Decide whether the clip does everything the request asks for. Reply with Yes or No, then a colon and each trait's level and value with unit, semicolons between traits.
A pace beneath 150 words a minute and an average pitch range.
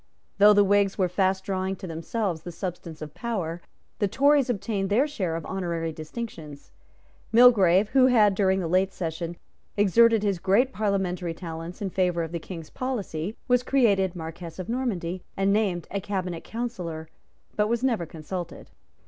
No: average, 165 wpm; average, 4.0 semitones